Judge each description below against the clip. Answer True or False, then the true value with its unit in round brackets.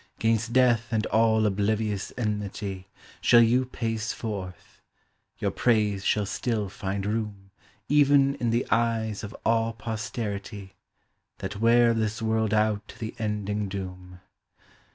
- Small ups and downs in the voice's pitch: True (2.1 semitones)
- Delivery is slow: True (130 wpm)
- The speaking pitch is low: True (110 Hz)